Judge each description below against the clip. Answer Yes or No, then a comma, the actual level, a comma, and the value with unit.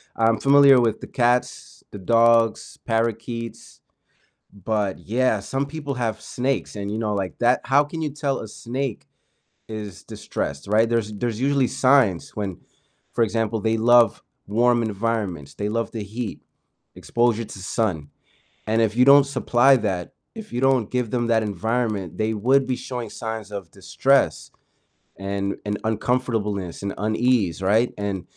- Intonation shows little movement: No, average, 3.2 semitones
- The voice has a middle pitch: No, low, 115 Hz